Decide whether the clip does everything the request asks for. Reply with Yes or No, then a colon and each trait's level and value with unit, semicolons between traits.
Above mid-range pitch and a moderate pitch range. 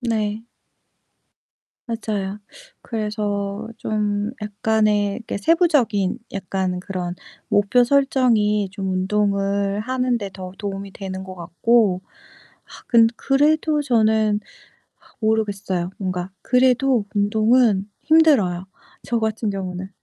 Yes: high, 210 Hz; average, 3.1 semitones